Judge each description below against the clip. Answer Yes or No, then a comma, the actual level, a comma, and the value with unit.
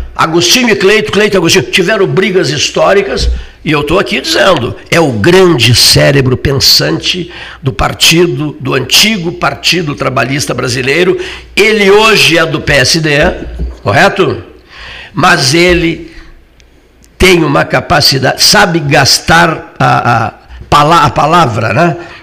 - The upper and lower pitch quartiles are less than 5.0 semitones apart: No, average, 5.3 semitones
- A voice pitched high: No, medium, 165 Hz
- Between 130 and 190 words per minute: No, slow, 120 wpm